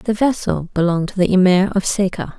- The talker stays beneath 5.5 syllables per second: No, 5.6 syllables/s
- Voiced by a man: No, female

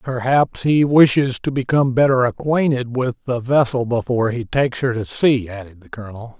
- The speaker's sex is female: No, male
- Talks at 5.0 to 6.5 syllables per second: Yes, 5.3 syllables/s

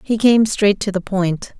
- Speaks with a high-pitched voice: Yes, high, 200 Hz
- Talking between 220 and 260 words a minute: Yes, fast, 225 wpm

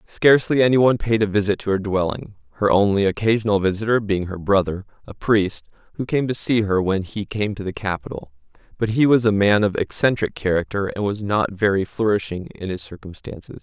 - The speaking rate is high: No, average, 195 wpm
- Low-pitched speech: Yes, low, 100 Hz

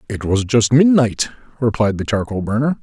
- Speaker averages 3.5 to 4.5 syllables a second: No, 5.2 syllables/s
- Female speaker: No, male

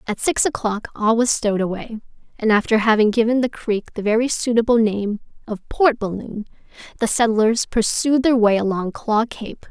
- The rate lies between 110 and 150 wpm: No, average, 175 wpm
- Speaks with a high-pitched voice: Yes, high, 225 Hz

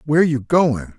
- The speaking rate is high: No, average, 185 wpm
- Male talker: Yes, male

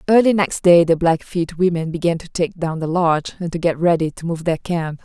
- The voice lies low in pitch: No, medium, 170 Hz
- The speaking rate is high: Yes, fast, 240 wpm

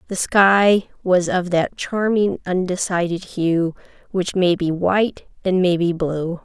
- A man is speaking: No, female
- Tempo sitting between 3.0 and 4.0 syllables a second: Yes, 3.8 syllables/s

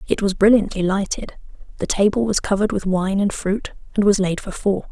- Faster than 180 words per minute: Yes, fast, 205 wpm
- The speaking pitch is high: Yes, high, 200 Hz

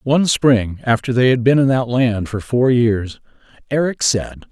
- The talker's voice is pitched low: Yes, low, 120 Hz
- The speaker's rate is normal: Yes, average, 185 wpm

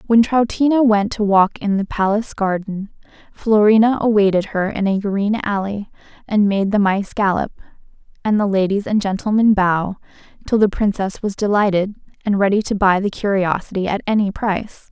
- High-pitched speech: Yes, high, 205 Hz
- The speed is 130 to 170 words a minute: Yes, average, 165 wpm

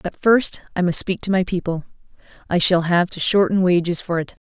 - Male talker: No, female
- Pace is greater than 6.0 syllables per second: No, 5.6 syllables/s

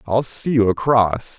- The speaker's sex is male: Yes, male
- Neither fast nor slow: Yes, average, 175 wpm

